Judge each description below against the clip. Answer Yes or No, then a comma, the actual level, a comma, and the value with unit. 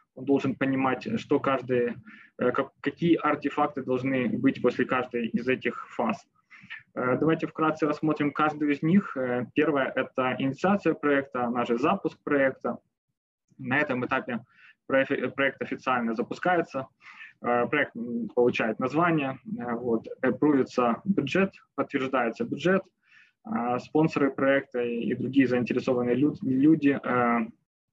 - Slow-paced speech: Yes, slow, 100 wpm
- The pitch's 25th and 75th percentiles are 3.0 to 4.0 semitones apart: Yes, average, 3.5 semitones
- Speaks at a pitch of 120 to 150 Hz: Yes, low, 135 Hz